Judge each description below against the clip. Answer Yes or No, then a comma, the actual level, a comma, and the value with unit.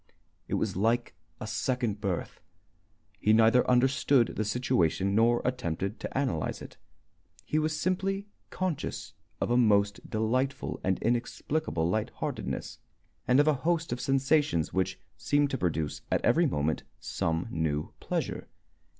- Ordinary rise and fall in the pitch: No, wide, 6.1 semitones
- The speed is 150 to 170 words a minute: No, average, 140 wpm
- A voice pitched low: Yes, low, 120 Hz